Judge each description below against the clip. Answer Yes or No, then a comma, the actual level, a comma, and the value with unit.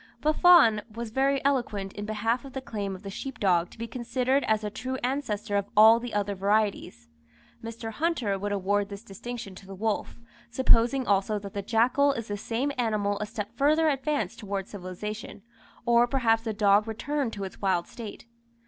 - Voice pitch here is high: Yes, high, 220 Hz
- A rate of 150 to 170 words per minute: No, average, 185 wpm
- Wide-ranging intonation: No, average, 3.7 semitones